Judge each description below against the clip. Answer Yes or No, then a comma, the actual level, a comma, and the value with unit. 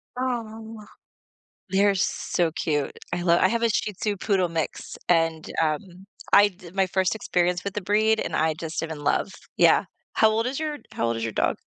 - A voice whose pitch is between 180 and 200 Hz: Yes, high, 190 Hz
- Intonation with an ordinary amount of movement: Yes, average, 4.7 semitones